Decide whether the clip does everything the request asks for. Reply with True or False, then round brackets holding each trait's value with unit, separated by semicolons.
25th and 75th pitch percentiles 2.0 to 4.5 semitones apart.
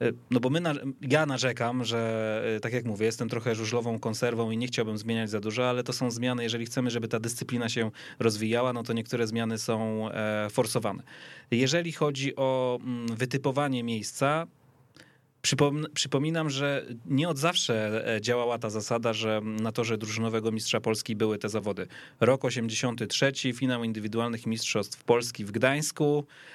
True (2.7 semitones)